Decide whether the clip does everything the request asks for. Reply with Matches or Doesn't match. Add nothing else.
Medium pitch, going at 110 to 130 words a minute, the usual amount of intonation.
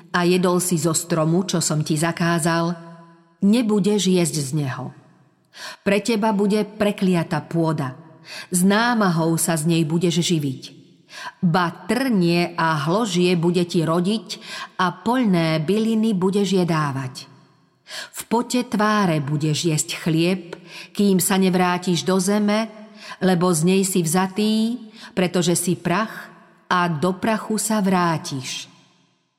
Matches